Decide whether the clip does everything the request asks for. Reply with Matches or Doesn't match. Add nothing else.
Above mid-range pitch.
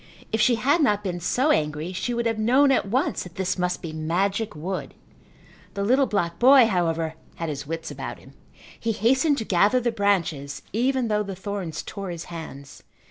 Matches